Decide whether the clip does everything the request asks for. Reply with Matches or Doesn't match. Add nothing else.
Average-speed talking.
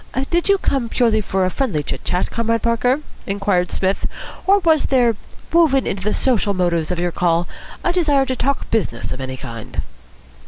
Matches